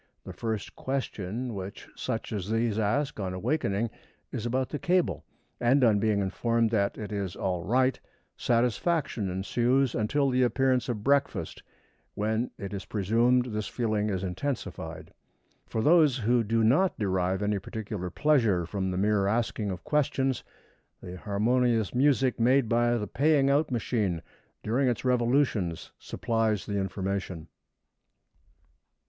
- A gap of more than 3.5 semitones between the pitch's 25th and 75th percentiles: Yes, average, 4.2 semitones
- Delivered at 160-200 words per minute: No, average, 140 wpm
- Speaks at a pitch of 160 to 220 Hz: No, low, 115 Hz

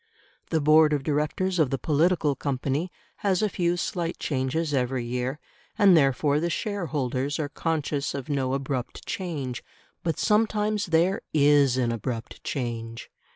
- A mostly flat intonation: No, average, 4.4 semitones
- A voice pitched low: No, medium, 145 Hz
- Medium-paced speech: Yes, average, 145 wpm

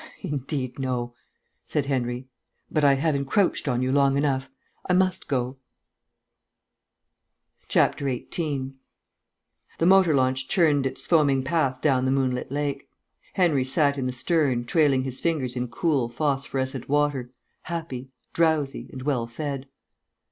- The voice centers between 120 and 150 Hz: Yes, low, 135 Hz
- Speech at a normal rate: No, slow, 130 wpm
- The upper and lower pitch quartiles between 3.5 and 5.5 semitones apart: No, narrow, 2.6 semitones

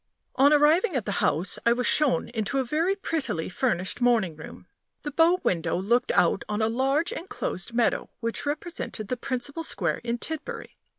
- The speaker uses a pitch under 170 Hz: No, high, 245 Hz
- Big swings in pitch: Yes, wide, 6.1 semitones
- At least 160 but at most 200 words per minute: Yes, average, 175 wpm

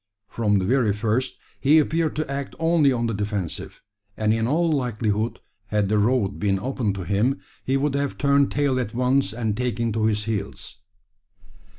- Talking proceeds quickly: No, average, 180 wpm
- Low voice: Yes, low, 115 Hz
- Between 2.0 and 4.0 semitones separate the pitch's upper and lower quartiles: No, average, 4.7 semitones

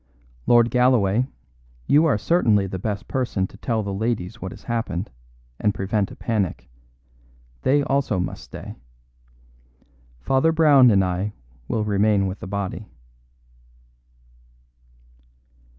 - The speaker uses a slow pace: Yes, slow, 120 wpm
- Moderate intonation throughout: Yes, average, 4.3 semitones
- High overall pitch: No, low, 105 Hz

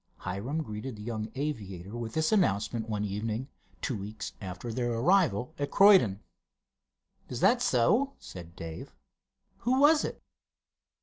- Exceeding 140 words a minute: No, slow, 135 wpm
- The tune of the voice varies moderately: No, wide, 7.3 semitones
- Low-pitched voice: Yes, low, 115 Hz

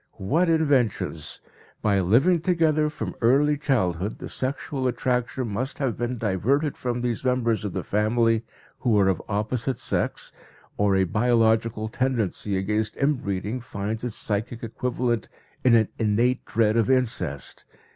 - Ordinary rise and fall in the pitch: Yes, average, 3.4 semitones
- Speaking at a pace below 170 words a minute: Yes, average, 145 wpm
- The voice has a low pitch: Yes, low, 115 Hz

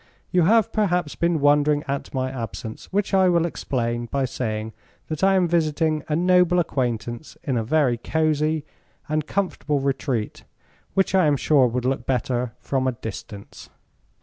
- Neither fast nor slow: Yes, average, 160 wpm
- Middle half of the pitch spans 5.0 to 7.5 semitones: Yes, average, 5.3 semitones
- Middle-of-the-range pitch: Yes, medium, 145 Hz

